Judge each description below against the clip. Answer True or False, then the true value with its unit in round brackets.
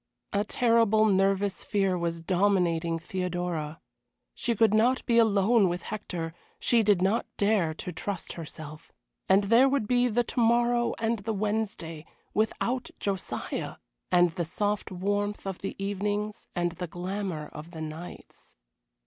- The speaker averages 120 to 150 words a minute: True (145 wpm)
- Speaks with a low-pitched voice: False (200 Hz)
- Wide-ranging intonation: False (3.7 semitones)